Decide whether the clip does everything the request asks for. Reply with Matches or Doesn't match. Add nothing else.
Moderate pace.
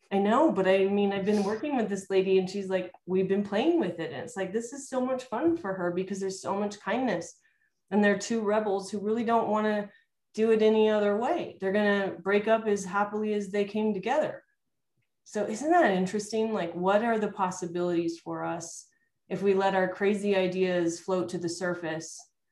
Doesn't match